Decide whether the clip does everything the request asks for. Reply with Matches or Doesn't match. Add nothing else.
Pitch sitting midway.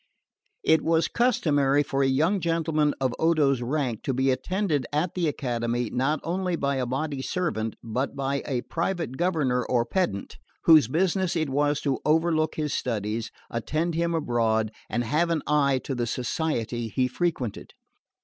Matches